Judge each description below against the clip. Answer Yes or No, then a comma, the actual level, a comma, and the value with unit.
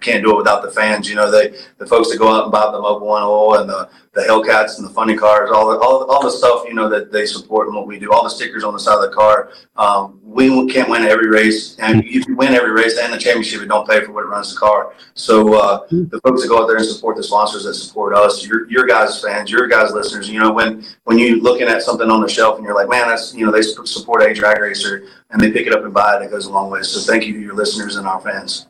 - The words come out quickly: Yes, fast, 300 wpm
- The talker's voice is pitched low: Yes, low, 110 Hz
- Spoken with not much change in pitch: Yes, narrow, 1.4 semitones